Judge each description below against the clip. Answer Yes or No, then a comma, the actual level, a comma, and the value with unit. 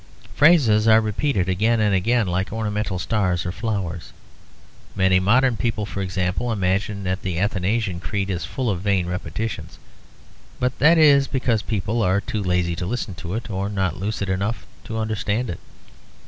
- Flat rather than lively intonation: No, average, 3.4 semitones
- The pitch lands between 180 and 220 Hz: No, low, 100 Hz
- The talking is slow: No, average, 165 wpm